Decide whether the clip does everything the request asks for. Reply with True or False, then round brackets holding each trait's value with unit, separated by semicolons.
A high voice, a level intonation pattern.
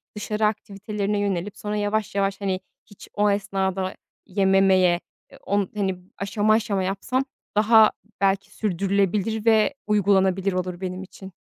True (200 Hz; 1.6 semitones)